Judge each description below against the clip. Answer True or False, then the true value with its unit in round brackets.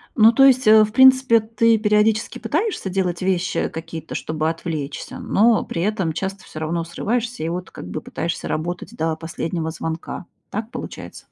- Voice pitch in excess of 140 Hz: True (190 Hz)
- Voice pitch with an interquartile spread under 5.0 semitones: False (5.4 semitones)